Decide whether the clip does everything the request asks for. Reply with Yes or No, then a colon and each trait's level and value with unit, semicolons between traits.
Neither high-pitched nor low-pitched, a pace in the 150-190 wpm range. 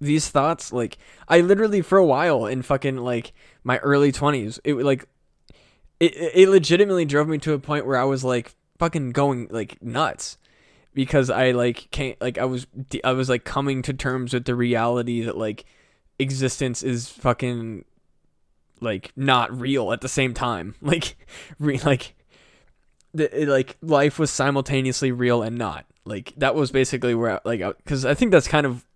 No: low, 130 Hz; average, 180 wpm